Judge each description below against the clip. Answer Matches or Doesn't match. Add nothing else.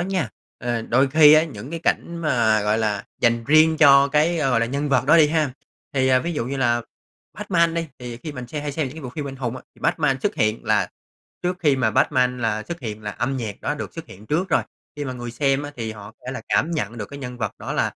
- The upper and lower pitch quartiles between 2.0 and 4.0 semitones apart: Doesn't match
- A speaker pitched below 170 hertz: Matches